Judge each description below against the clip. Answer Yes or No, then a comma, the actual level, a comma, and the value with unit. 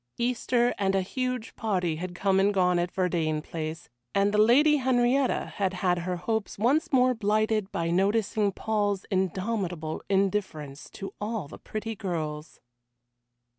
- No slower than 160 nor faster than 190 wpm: No, average, 145 wpm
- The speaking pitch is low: No, high, 195 Hz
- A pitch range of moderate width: Yes, average, 3.9 semitones